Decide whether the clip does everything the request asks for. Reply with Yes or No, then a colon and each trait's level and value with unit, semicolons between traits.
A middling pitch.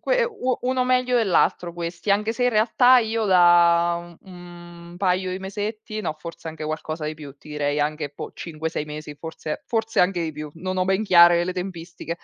Yes: medium, 175 Hz